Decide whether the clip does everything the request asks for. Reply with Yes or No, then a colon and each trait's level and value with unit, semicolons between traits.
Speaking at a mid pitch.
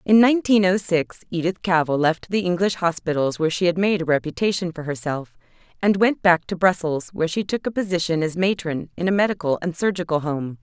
Yes: medium, 175 Hz